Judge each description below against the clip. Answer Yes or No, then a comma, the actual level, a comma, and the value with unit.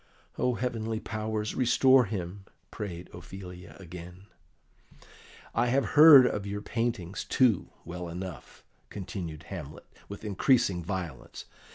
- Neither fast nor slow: No, slow, 110 wpm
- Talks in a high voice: No, low, 100 Hz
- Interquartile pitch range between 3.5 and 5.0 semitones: Yes, average, 4.5 semitones